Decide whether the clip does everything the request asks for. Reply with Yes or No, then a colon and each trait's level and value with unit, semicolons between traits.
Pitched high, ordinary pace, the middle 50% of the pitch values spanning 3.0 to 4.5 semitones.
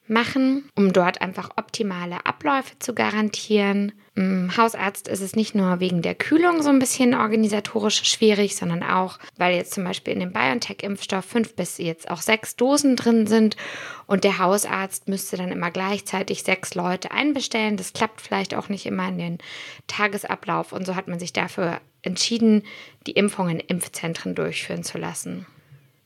Yes: high, 200 Hz; average, 165 wpm; average, 3.4 semitones